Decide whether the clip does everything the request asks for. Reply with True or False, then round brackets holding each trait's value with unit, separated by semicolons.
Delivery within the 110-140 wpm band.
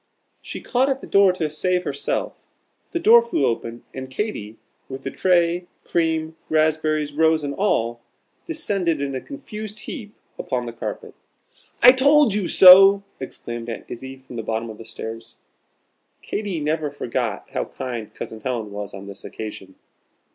False (160 wpm)